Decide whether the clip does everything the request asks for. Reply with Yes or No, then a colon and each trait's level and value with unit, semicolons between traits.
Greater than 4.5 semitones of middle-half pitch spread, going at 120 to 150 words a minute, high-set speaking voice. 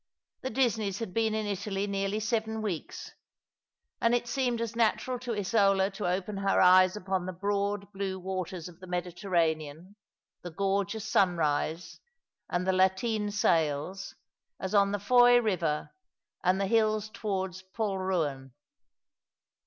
No: average, 2.9 semitones; average, 140 wpm; high, 195 Hz